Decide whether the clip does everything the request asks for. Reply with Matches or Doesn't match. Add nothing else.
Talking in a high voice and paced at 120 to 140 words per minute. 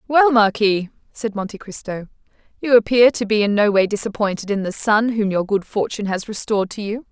Doesn't match